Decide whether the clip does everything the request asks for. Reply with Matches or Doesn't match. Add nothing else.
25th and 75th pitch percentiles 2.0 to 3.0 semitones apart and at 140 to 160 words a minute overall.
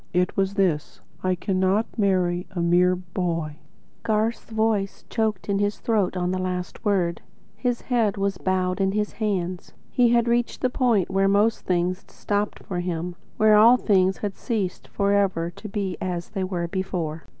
Doesn't match